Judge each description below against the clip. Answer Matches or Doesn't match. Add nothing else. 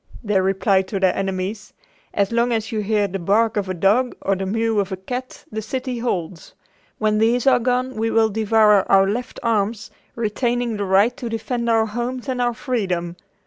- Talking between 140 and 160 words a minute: Doesn't match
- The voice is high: Matches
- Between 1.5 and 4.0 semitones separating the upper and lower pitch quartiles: Matches